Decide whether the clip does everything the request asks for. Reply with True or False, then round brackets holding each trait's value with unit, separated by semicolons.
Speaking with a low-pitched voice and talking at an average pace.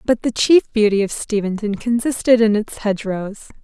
False (220 Hz; 165 wpm)